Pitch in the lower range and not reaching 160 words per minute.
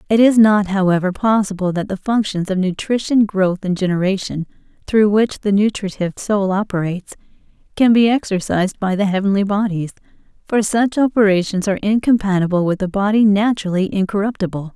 No: high, 200 Hz; average, 145 wpm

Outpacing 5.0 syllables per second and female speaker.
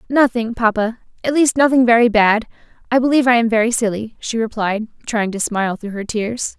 Yes: 5.6 syllables/s; female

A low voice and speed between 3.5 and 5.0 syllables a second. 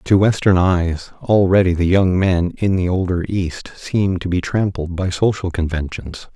Yes: very low, 90 Hz; 4.5 syllables/s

